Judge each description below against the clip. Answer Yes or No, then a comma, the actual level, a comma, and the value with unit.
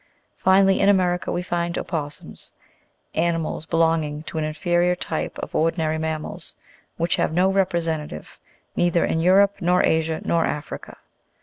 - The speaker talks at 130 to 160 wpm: Yes, average, 140 wpm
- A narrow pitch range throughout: Yes, narrow, 2.1 semitones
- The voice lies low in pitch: No, medium, 170 Hz